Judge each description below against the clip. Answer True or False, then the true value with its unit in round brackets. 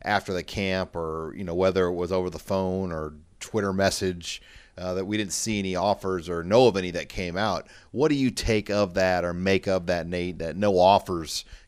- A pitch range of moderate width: False (1.9 semitones)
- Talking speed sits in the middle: False (220 wpm)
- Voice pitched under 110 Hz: True (95 Hz)